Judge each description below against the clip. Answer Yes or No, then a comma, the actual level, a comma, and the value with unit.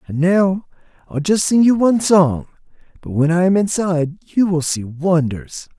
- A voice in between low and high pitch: Yes, medium, 170 Hz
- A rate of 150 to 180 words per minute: Yes, average, 175 wpm